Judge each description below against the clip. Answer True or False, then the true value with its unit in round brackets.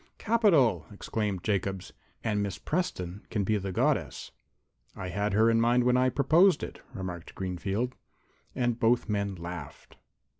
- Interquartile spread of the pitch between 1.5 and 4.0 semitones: False (4.5 semitones)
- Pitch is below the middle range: True (105 Hz)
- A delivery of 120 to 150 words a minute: True (145 wpm)